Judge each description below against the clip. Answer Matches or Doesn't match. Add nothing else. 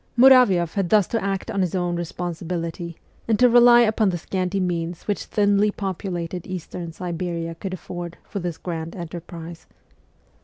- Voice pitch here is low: Doesn't match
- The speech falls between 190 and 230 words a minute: Doesn't match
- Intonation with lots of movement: Doesn't match